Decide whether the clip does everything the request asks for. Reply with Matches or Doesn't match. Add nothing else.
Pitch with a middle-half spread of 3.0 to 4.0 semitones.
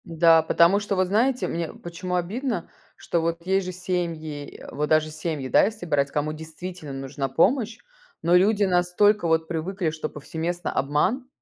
Matches